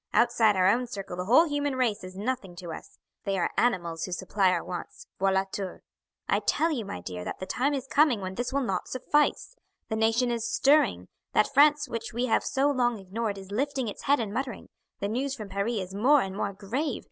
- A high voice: Yes, high, 225 Hz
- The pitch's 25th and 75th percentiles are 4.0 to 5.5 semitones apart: Yes, average, 5.2 semitones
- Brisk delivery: Yes, fast, 220 wpm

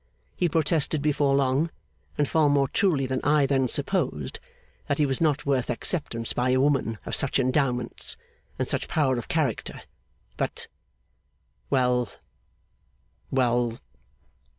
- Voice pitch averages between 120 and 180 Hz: Yes, low, 135 Hz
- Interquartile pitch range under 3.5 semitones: Yes, average, 2.8 semitones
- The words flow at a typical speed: No, slow, 130 wpm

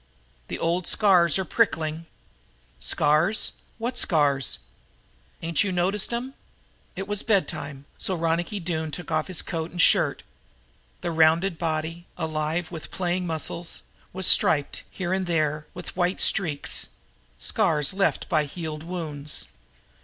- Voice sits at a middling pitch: Yes, medium, 170 Hz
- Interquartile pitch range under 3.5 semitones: Yes, average, 2.9 semitones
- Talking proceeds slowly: Yes, slow, 130 wpm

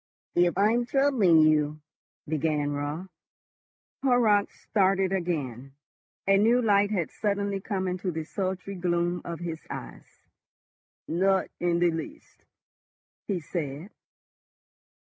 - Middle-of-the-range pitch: Yes, medium, 180 Hz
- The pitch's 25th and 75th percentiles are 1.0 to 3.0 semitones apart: No, average, 3.8 semitones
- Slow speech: Yes, slow, 115 wpm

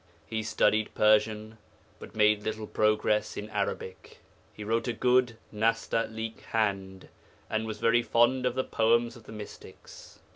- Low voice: Yes, low, 110 Hz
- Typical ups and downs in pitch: No, narrow, 1.3 semitones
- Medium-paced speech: Yes, average, 145 wpm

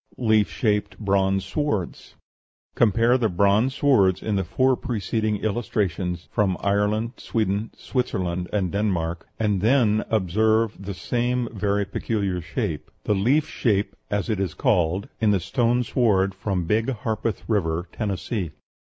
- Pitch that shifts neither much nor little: Yes, average, 3.1 semitones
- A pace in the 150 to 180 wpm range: No, slow, 135 wpm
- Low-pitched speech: Yes, low, 105 Hz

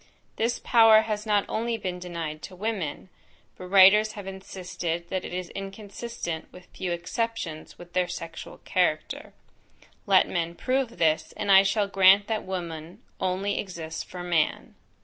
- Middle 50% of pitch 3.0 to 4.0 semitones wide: Yes, average, 3.4 semitones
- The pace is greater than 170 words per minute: No, average, 155 wpm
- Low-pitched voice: No, high, 190 Hz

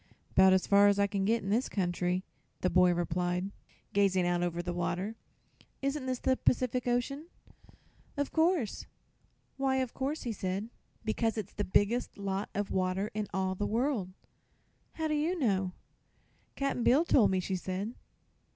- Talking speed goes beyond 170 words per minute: No, average, 165 wpm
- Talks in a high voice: Yes, high, 205 Hz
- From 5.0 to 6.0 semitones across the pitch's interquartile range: Yes, average, 5.3 semitones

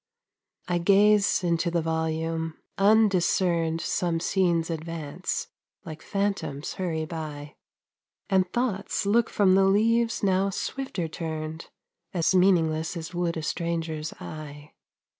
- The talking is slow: Yes, slow, 115 wpm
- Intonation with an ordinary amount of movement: Yes, average, 3.3 semitones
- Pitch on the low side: No, medium, 170 Hz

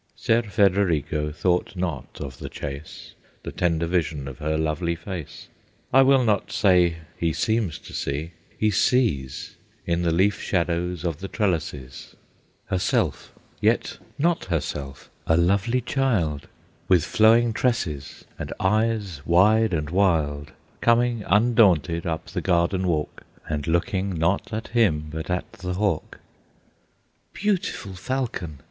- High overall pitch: No, very low, 90 Hz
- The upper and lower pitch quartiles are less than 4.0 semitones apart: No, average, 5.0 semitones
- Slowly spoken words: Yes, slow, 130 wpm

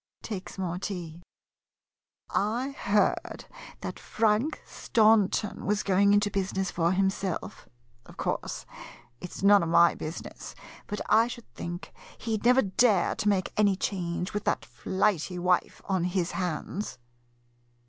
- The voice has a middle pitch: No, high, 195 Hz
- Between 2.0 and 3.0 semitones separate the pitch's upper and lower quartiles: Yes, average, 2.7 semitones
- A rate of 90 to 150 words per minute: Yes, average, 140 wpm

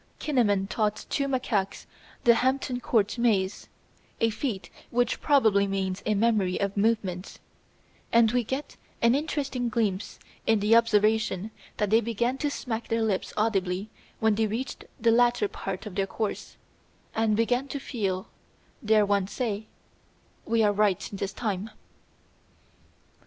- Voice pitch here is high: Yes, high, 220 Hz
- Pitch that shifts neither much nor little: Yes, average, 3.0 semitones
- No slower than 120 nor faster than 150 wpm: Yes, average, 140 wpm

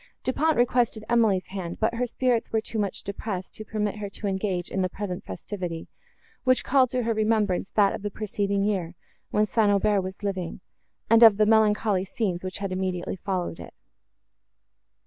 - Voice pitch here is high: Yes, high, 205 Hz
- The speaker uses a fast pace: No, average, 185 wpm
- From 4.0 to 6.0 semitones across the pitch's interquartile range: No, average, 2.8 semitones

